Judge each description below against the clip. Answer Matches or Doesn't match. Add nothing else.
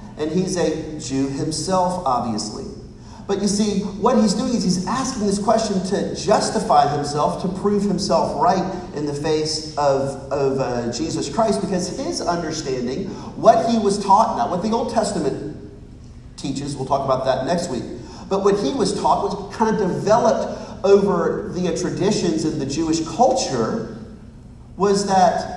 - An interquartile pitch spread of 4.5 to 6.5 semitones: Matches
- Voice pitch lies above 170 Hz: Matches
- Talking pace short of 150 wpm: Doesn't match